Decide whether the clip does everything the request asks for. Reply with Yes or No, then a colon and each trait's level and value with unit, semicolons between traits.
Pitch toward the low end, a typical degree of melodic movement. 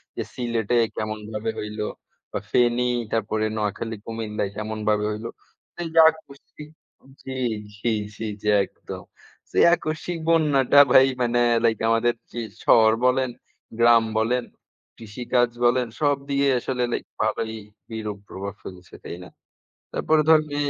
Yes: low, 115 Hz; average, 3.4 semitones